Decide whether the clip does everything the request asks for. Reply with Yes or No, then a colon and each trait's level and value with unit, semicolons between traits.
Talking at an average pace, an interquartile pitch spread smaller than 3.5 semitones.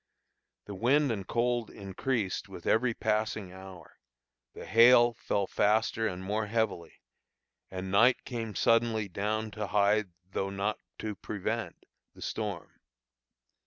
No: slow, 125 wpm; average, 2.8 semitones